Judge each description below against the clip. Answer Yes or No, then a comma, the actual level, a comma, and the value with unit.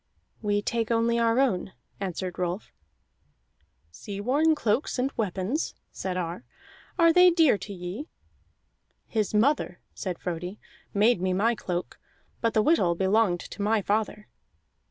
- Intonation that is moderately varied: Yes, average, 4.3 semitones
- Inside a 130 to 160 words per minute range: Yes, slow, 135 wpm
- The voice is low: No, high, 210 Hz